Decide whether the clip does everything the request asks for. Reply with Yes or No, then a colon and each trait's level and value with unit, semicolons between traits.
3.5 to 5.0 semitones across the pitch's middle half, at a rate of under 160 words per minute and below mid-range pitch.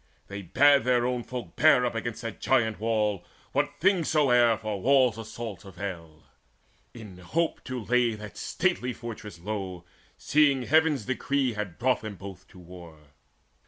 Yes: average, 4.5 semitones; average, 150 wpm; low, 115 Hz